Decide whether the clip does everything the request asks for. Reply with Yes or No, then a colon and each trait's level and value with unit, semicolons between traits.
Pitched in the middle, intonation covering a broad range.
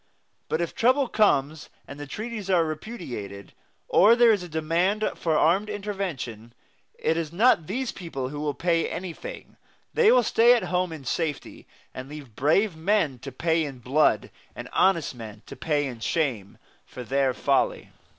Yes: medium, 160 Hz; wide, 6.5 semitones